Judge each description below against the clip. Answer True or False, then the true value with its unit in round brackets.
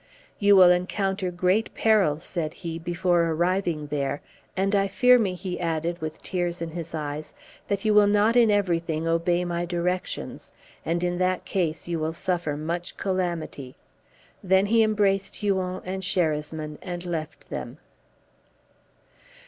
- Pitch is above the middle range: False (175 Hz)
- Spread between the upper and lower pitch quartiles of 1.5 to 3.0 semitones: True (2.7 semitones)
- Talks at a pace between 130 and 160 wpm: True (150 wpm)